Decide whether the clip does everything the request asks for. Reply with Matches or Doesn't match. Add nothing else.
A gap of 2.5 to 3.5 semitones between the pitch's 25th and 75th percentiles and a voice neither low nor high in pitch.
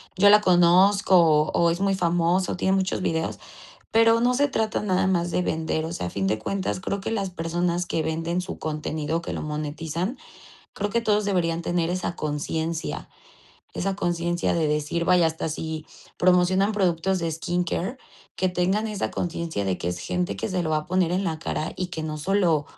Matches